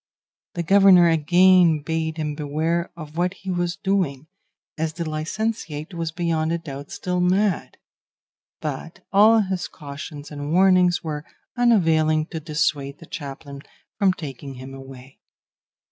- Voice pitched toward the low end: No, medium, 165 Hz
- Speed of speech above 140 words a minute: No, slow, 135 wpm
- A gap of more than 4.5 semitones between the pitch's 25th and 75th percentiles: No, average, 3.4 semitones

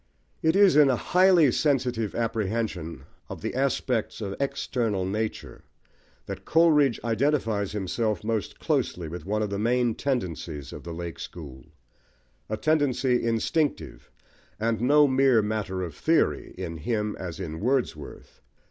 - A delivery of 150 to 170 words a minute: No, average, 140 wpm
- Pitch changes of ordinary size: No, wide, 5.9 semitones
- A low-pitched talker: Yes, low, 110 Hz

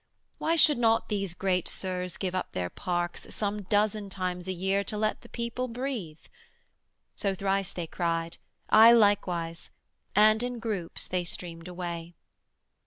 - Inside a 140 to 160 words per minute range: Yes, average, 150 wpm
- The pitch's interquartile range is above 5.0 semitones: No, average, 3.6 semitones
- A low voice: No, high, 195 Hz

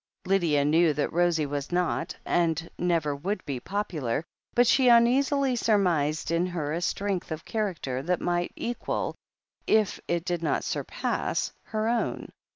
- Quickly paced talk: No, average, 150 wpm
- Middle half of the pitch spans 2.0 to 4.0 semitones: No, average, 5.0 semitones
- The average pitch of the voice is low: No, medium, 175 Hz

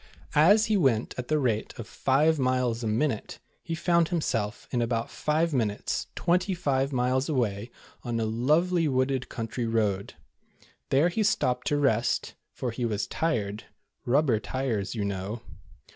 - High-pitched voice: No, low, 125 Hz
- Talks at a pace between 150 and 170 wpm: Yes, average, 160 wpm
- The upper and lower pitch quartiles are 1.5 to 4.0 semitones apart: No, average, 5.2 semitones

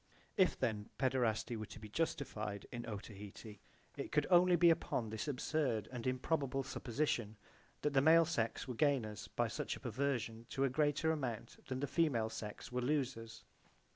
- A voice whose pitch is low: Yes, low, 125 Hz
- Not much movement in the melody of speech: No, average, 4.8 semitones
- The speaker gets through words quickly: No, average, 170 wpm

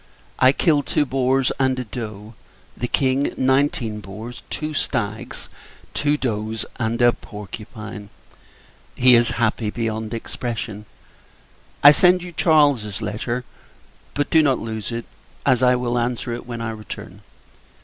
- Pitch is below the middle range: Yes, low, 120 Hz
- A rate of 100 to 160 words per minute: Yes, average, 140 wpm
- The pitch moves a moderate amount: Yes, average, 3.2 semitones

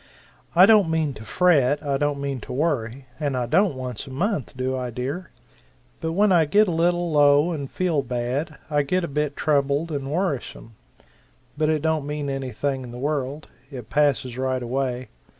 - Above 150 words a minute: Yes, average, 185 wpm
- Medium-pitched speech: Yes, medium, 145 Hz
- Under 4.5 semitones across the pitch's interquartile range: Yes, average, 3.6 semitones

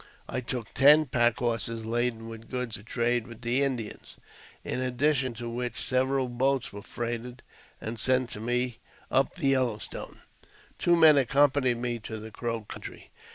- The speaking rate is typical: Yes, average, 165 wpm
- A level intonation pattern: Yes, narrow, 2.1 semitones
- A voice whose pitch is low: Yes, low, 120 Hz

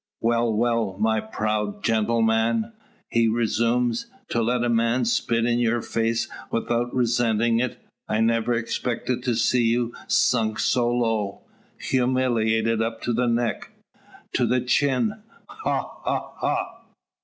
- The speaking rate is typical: No, slow, 130 wpm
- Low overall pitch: Yes, low, 115 Hz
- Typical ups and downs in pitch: No, narrow, 1.3 semitones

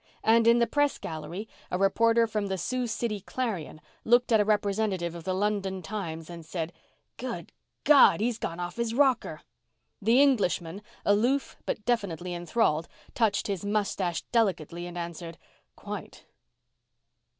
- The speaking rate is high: No, average, 145 wpm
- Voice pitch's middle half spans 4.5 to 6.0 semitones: Yes, average, 4.9 semitones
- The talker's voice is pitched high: Yes, high, 205 Hz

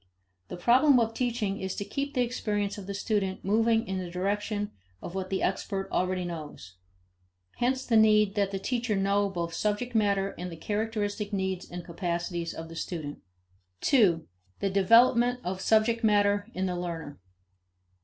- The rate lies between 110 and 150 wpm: No, average, 170 wpm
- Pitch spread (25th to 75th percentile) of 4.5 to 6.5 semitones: No, average, 3.4 semitones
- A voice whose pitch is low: No, high, 200 Hz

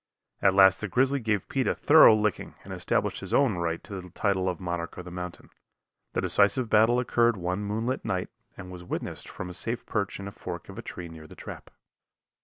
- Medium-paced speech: No, fast, 215 wpm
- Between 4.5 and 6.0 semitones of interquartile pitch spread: No, average, 3.9 semitones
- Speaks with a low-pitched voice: Yes, low, 100 Hz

